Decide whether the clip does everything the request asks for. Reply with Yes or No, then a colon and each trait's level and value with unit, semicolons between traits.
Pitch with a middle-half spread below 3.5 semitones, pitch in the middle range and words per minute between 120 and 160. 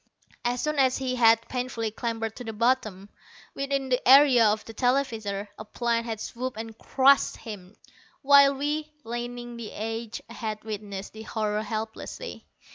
No: average, 3.0 semitones; high, 230 Hz; average, 155 wpm